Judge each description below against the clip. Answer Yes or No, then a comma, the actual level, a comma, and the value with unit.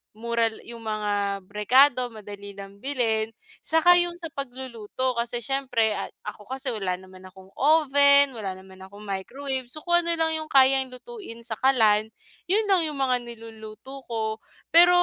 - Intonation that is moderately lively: Yes, average, 4.7 semitones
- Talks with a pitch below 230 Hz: No, high, 240 Hz